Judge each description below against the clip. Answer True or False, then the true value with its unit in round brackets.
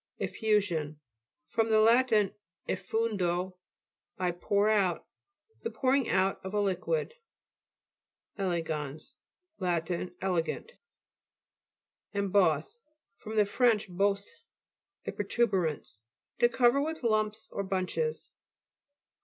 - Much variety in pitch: False (4.1 semitones)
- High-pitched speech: True (200 Hz)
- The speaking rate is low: True (95 wpm)